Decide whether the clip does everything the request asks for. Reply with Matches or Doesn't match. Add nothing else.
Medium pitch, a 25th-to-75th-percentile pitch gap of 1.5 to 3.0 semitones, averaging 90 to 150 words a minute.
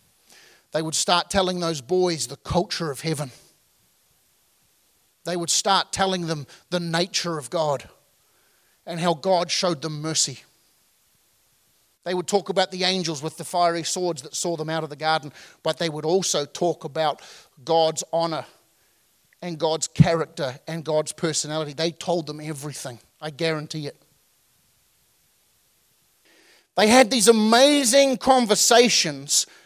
Matches